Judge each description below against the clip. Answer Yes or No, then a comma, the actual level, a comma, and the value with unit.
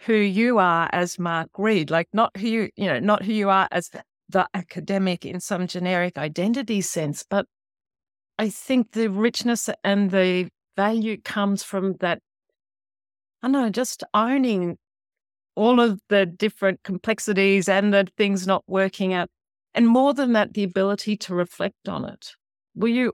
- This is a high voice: Yes, high, 200 Hz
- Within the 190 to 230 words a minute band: No, average, 165 wpm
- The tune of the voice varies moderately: Yes, average, 3.2 semitones